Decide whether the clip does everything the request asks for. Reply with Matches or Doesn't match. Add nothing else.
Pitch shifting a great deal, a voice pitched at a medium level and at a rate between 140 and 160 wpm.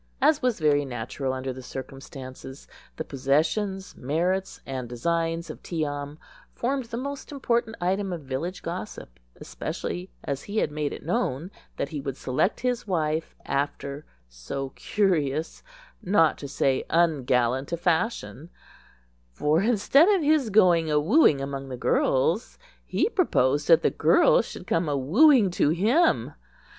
Matches